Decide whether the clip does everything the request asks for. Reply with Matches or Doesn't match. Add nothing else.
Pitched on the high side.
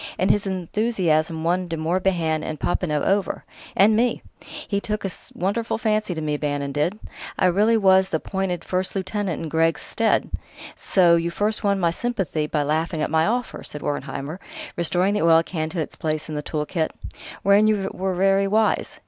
Doesn't match